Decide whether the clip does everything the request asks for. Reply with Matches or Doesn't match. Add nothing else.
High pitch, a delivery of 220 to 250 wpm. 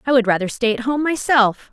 Matches